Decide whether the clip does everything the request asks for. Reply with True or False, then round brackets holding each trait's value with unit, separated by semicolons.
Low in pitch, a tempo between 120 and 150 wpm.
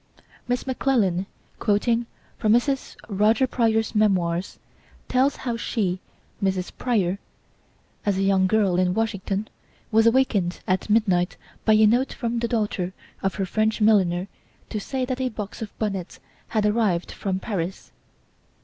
False (210 Hz; 140 wpm)